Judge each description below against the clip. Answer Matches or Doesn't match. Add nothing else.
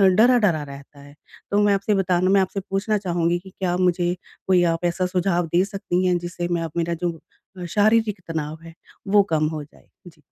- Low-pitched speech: Doesn't match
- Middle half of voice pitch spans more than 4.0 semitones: Doesn't match